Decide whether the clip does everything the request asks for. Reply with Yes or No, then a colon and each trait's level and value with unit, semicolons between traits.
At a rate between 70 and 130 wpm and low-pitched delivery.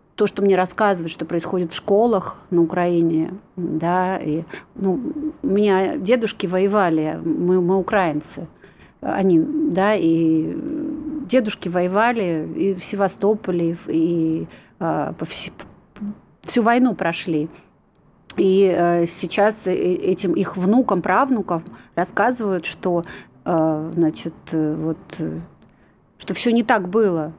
No: slow, 110 wpm; medium, 185 Hz